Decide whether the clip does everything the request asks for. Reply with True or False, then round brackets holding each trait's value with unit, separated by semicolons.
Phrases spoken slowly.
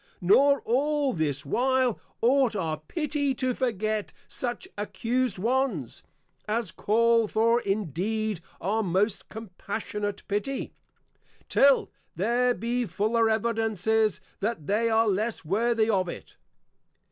True (110 wpm)